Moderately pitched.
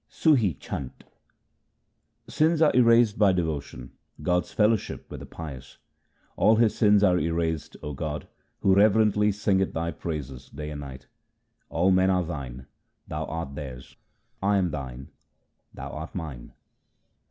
No: very low, 85 Hz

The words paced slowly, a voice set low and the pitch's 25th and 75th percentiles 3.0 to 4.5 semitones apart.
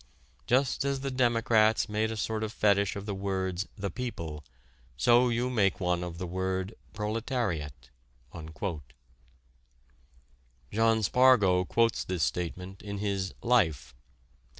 Yes: slow, 125 wpm; low, 100 Hz; average, 3.9 semitones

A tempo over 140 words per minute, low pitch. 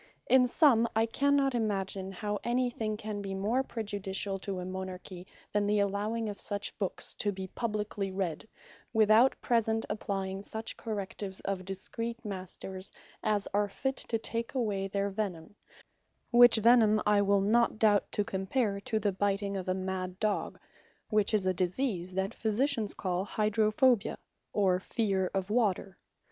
No: average, 155 wpm; high, 205 Hz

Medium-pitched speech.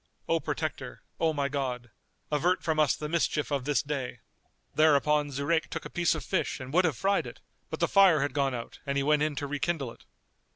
Yes: medium, 145 Hz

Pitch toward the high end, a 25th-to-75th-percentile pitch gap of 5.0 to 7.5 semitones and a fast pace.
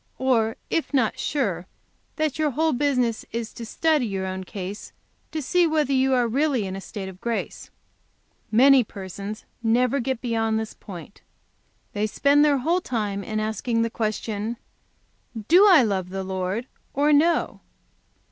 No: high, 230 Hz; average, 5.3 semitones; average, 155 wpm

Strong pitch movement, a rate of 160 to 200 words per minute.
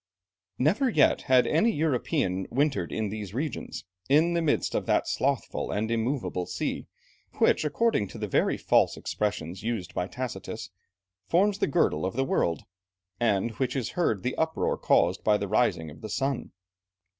Yes: wide, 7.0 semitones; average, 170 wpm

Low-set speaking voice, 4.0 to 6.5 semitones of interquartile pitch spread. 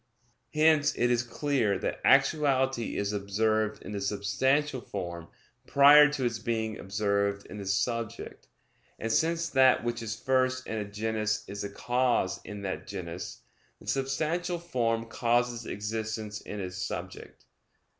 Yes: low, 115 Hz; average, 4.5 semitones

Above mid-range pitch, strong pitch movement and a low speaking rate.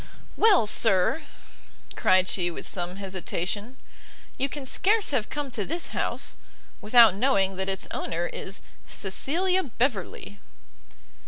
Yes: high, 210 Hz; wide, 6.5 semitones; slow, 120 wpm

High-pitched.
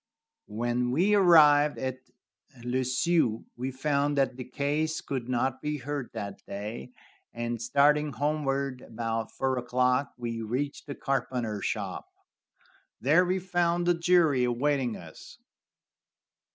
No: low, 135 Hz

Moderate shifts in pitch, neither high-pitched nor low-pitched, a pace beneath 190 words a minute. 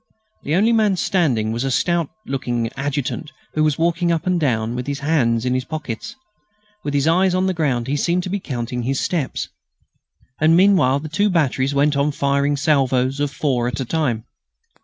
No: average, 4.6 semitones; medium, 145 Hz; average, 195 wpm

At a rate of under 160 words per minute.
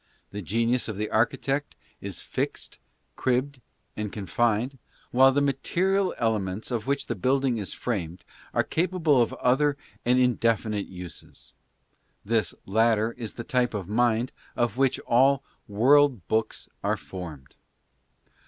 Yes: average, 145 wpm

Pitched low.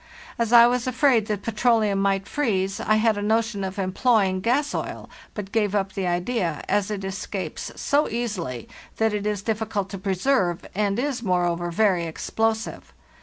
No: high, 210 Hz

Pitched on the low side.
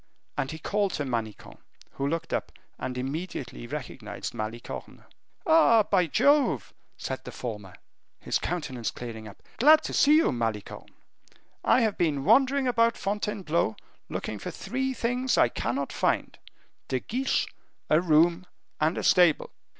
No: medium, 165 Hz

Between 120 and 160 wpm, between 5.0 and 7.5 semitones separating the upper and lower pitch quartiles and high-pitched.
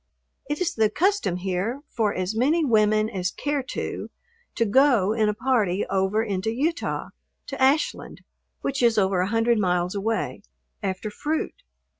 Yes: average, 155 wpm; wide, 5.4 semitones; high, 220 Hz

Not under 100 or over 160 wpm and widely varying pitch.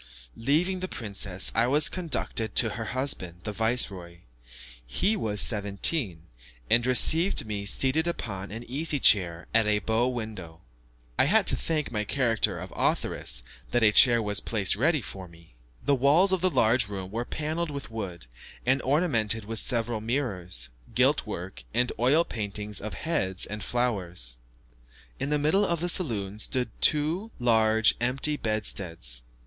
Yes: average, 155 wpm; wide, 5.8 semitones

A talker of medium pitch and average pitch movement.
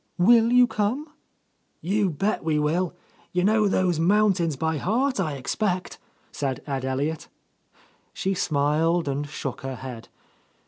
No: medium, 175 Hz; wide, 6.1 semitones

